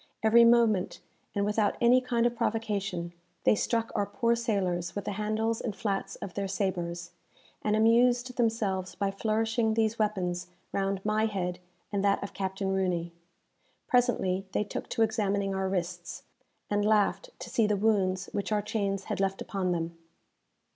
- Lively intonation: No, average, 2.7 semitones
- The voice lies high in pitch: Yes, high, 205 Hz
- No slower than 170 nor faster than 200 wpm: No, average, 160 wpm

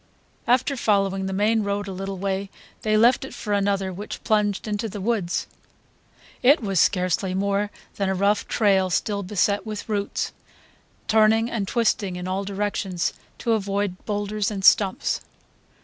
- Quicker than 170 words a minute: No, average, 155 wpm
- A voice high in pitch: Yes, high, 200 Hz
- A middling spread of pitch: No, narrow, 1.8 semitones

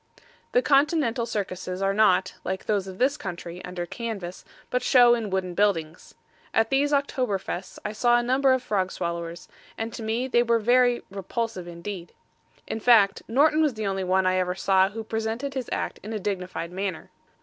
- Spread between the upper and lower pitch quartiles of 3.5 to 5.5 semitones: Yes, average, 4.6 semitones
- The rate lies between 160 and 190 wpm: Yes, average, 185 wpm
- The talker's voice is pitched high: Yes, high, 210 Hz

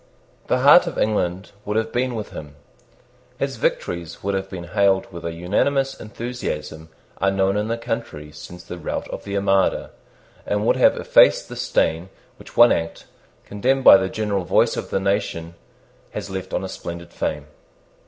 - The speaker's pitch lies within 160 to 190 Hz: No, very low, 95 Hz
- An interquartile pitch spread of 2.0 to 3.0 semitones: No, average, 4.2 semitones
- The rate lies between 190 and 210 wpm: No, average, 175 wpm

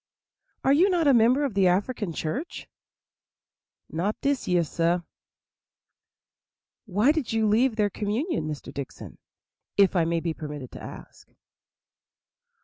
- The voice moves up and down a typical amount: No, wide, 7.5 semitones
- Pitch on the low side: No, high, 205 Hz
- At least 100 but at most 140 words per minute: Yes, slow, 135 wpm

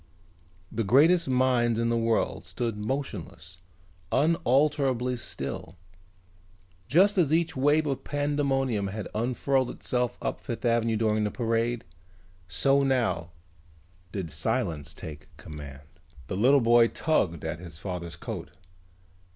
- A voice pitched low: Yes, low, 120 Hz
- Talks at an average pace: No, slow, 120 wpm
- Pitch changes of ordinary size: No, wide, 5.8 semitones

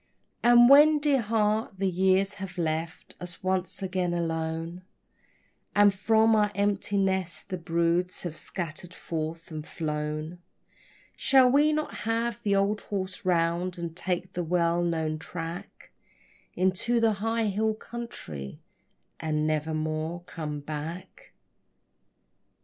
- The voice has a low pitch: No, medium, 180 Hz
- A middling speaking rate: No, slow, 125 wpm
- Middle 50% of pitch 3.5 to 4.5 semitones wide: Yes, average, 4.1 semitones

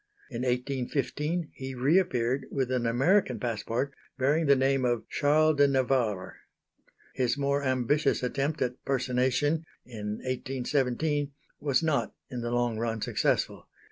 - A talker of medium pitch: No, low, 130 Hz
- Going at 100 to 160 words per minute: Yes, slow, 135 wpm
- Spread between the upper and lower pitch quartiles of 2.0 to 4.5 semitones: Yes, average, 2.7 semitones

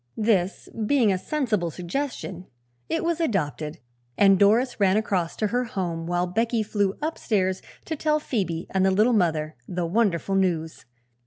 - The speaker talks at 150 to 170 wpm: Yes, average, 155 wpm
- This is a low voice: No, high, 195 Hz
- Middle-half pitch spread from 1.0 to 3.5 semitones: No, average, 4.7 semitones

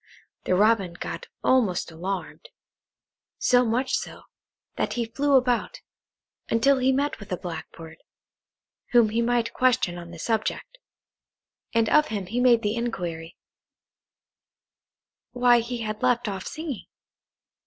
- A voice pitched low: No, high, 230 Hz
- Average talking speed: No, slow, 130 wpm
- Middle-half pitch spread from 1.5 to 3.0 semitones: No, average, 4.7 semitones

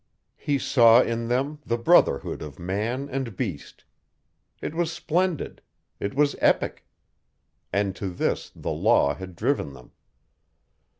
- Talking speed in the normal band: No, slow, 130 wpm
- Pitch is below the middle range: Yes, low, 115 Hz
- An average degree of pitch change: No, wide, 7.1 semitones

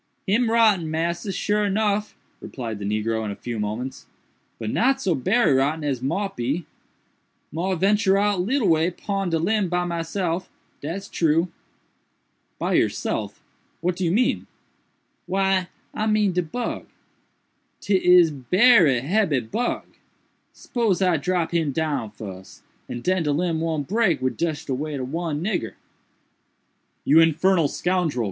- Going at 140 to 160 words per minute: Yes, average, 145 wpm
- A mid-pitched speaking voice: Yes, medium, 170 Hz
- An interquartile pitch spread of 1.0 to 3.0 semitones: No, average, 5.2 semitones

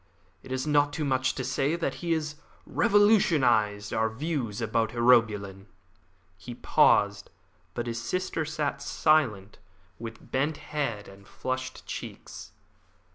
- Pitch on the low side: Yes, low, 130 Hz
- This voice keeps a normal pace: No, slow, 130 wpm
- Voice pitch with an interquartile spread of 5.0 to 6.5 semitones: Yes, average, 5.3 semitones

